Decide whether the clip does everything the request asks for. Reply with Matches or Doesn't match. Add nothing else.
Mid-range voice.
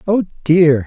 Matches